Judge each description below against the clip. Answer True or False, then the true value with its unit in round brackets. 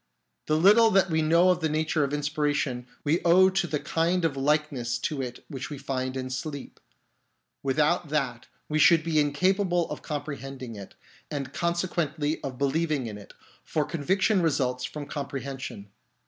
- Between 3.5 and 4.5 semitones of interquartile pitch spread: True (3.8 semitones)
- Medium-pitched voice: True (150 Hz)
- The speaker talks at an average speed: True (165 wpm)